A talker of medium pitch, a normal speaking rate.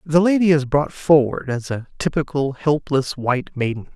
Yes: medium, 145 Hz; average, 165 wpm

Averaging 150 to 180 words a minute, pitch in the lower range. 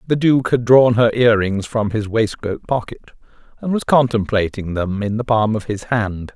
No: average, 200 wpm; low, 115 Hz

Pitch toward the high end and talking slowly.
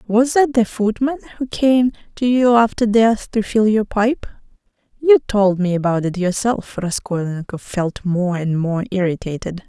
No: high, 210 Hz; average, 160 wpm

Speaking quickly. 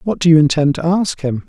Yes: fast, 285 wpm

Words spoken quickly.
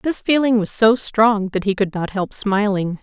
Yes: fast, 220 wpm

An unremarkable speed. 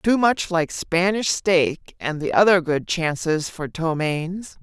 Yes: average, 155 wpm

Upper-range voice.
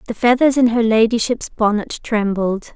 Yes: high, 225 Hz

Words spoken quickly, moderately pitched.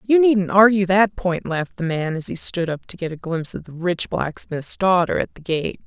Yes: fast, 245 wpm; medium, 180 Hz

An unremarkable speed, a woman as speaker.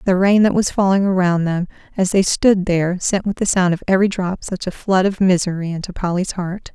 No: fast, 230 wpm; female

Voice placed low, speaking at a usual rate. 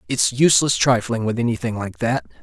Yes: low, 120 Hz; average, 175 wpm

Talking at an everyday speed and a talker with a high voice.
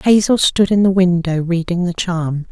No: average, 190 wpm; medium, 180 Hz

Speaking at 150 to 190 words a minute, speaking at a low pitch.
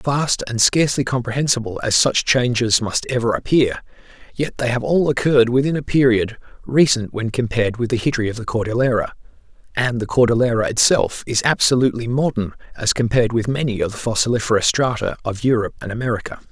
Yes: average, 165 wpm; low, 120 Hz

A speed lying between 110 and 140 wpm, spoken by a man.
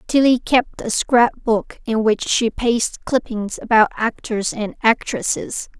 No: slow, 135 wpm; female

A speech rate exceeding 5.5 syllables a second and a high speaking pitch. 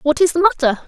Yes: 6.1 syllables/s; very high, 305 Hz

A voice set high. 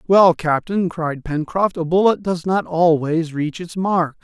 No: medium, 170 Hz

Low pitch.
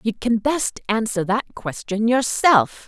No: high, 225 Hz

